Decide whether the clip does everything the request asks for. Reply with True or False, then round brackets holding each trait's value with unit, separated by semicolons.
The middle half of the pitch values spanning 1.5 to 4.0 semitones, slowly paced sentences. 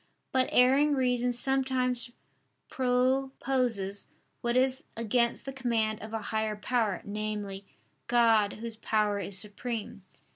True (3.1 semitones; 115 wpm)